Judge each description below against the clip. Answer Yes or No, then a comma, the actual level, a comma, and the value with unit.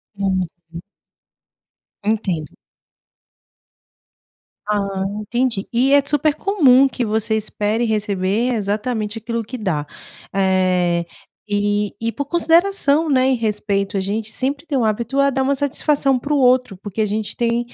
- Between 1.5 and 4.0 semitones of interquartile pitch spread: No, average, 4.7 semitones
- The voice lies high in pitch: Yes, high, 225 Hz